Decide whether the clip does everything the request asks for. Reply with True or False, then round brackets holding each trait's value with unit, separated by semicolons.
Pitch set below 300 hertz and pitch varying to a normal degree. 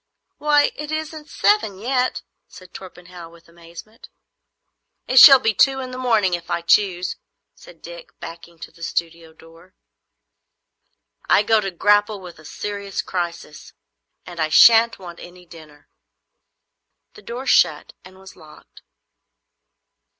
False (190 Hz; 6.3 semitones)